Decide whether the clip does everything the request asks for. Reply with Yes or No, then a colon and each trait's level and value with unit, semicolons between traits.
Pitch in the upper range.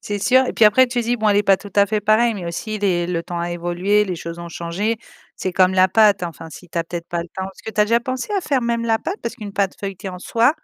Yes: high, 200 Hz